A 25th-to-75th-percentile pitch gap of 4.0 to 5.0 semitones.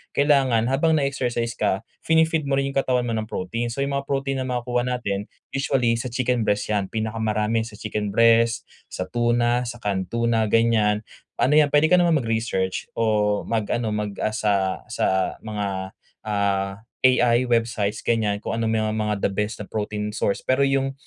No: average, 3.3 semitones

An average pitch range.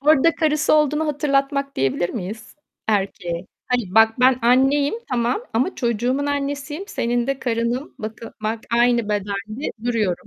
Yes: average, 4.2 semitones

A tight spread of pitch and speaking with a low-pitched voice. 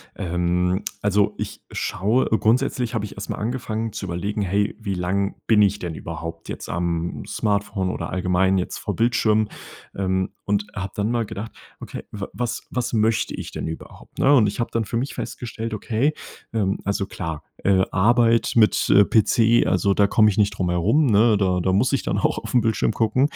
No: average, 3.2 semitones; low, 105 Hz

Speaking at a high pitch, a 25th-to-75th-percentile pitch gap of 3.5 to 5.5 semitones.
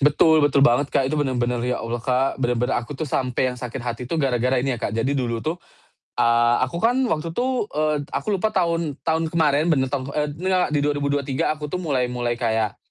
No: medium, 140 Hz; average, 4.0 semitones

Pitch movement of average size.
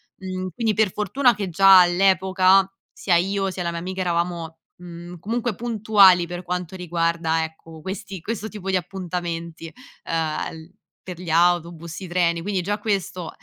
No: narrow, 2.3 semitones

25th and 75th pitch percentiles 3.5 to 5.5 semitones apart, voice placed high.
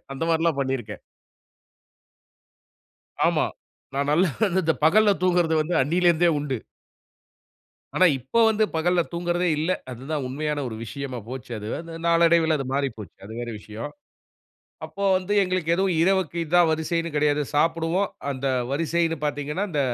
No: average, 3.8 semitones; medium, 160 Hz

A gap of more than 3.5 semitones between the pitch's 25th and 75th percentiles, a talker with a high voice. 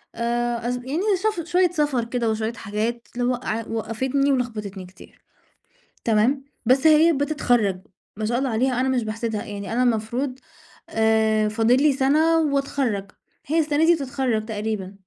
Yes: average, 4.0 semitones; high, 240 Hz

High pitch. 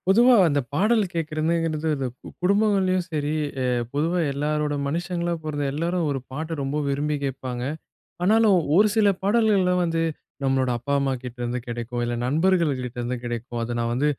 No: medium, 150 Hz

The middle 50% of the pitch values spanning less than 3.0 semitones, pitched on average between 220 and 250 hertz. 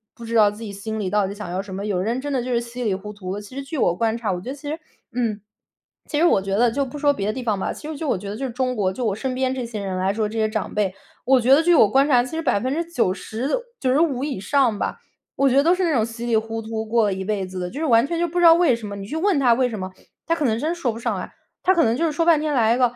No: average, 5.0 semitones; high, 235 Hz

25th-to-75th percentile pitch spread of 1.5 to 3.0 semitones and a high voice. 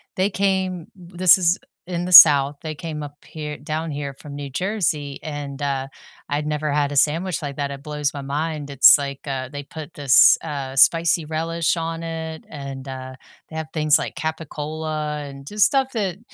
No: narrow, 2.6 semitones; medium, 150 Hz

